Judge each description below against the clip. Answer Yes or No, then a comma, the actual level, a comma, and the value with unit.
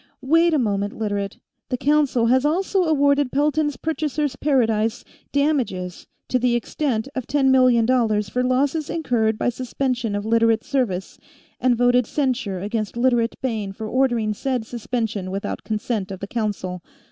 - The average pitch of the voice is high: Yes, high, 245 Hz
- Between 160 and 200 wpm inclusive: No, average, 150 wpm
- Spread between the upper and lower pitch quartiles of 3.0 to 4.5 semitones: Yes, average, 4.1 semitones